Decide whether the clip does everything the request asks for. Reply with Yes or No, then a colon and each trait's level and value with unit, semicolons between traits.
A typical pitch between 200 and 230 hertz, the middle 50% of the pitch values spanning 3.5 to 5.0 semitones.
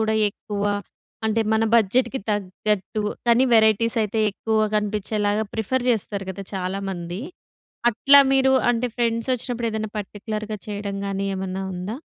No: high, 215 Hz; narrow, 2.5 semitones